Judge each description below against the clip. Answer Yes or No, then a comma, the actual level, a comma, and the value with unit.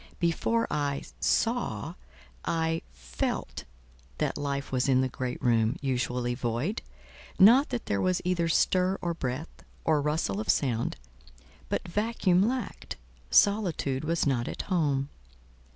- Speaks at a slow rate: Yes, slow, 130 wpm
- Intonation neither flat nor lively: No, wide, 6.5 semitones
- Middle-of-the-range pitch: Yes, medium, 150 Hz